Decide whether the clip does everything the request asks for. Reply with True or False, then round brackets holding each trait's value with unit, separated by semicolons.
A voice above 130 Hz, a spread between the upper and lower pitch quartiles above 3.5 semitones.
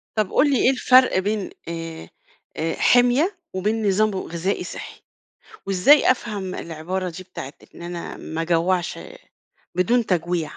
True (185 Hz; 4.4 semitones)